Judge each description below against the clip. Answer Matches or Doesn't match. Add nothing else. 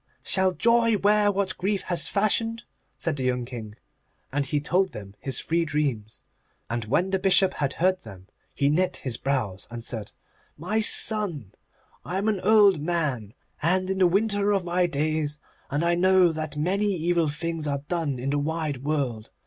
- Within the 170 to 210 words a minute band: Matches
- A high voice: Doesn't match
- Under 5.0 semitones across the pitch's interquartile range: Doesn't match